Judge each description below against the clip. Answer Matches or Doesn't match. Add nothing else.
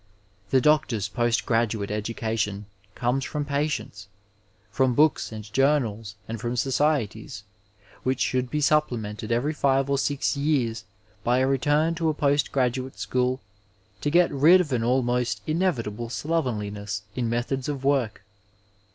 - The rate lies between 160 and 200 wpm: Doesn't match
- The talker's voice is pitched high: Doesn't match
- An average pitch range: Matches